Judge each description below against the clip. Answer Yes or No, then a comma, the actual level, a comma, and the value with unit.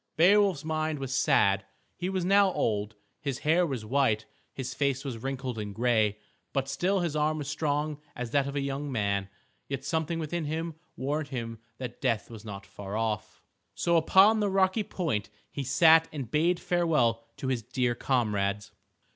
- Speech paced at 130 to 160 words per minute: No, average, 175 wpm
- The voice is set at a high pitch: No, medium, 140 Hz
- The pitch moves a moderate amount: No, wide, 5.9 semitones